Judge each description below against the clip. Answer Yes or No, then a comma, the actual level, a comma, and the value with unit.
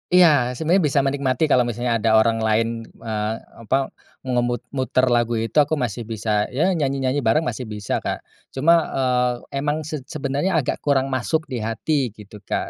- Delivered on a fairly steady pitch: No, average, 3.9 semitones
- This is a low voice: Yes, low, 125 Hz